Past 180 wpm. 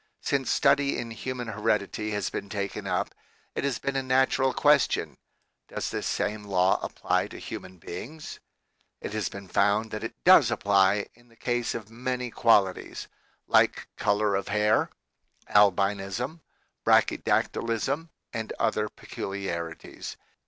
No: slow, 135 wpm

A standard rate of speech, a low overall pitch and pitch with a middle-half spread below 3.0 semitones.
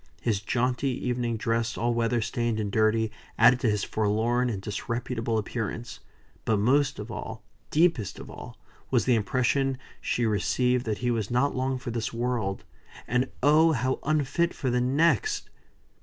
Yes: average, 160 wpm; low, 120 Hz; narrow, 2.5 semitones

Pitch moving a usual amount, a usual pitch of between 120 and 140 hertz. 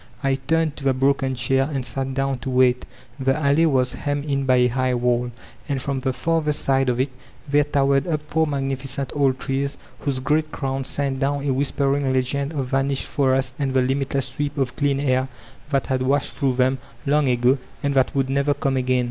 No: narrow, 1.4 semitones; low, 135 Hz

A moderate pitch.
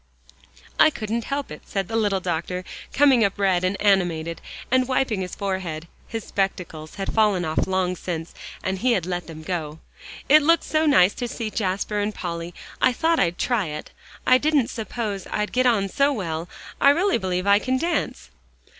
No: high, 200 Hz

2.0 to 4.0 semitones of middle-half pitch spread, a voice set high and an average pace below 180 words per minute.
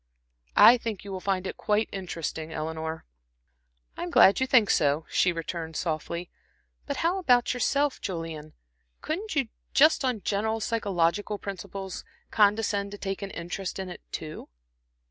No: average, 5.0 semitones; high, 195 Hz; average, 150 wpm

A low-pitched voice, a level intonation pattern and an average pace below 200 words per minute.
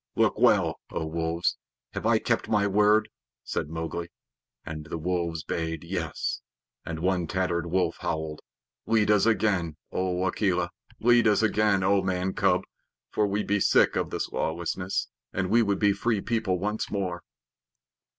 No: very low, 95 Hz; average, 3.5 semitones; average, 160 wpm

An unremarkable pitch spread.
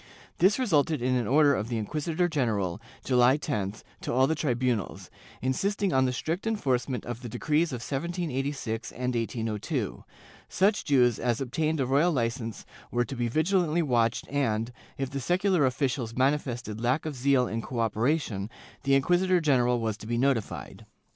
Yes: average, 4.5 semitones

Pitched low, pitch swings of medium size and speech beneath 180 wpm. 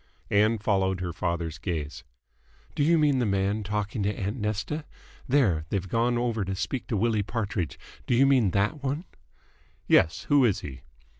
Yes: low, 105 Hz; average, 4.3 semitones; average, 170 wpm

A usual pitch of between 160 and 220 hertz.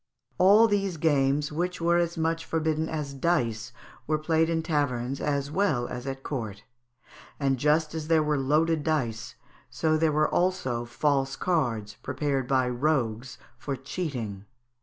No: medium, 150 Hz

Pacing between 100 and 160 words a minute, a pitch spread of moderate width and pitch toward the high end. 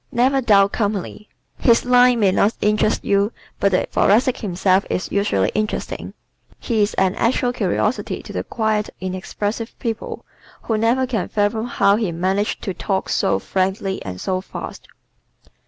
Yes: average, 155 wpm; average, 3.1 semitones; high, 210 Hz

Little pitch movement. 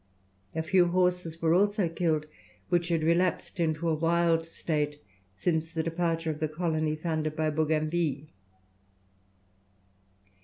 Yes: narrow, 1.7 semitones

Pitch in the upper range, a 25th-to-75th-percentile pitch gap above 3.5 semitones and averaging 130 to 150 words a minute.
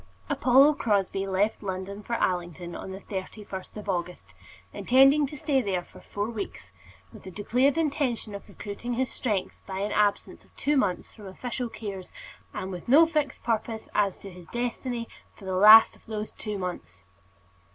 No: high, 210 Hz; average, 4.4 semitones; average, 170 wpm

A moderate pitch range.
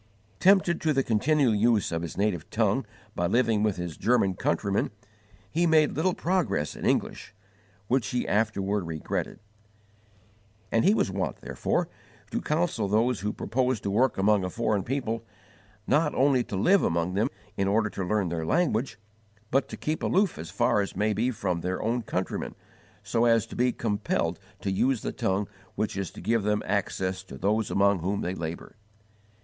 Yes: average, 4.7 semitones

